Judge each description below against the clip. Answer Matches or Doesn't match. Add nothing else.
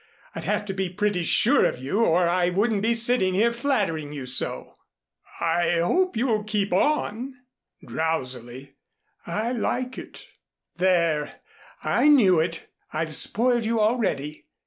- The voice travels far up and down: Matches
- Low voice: Doesn't match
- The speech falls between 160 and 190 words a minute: Doesn't match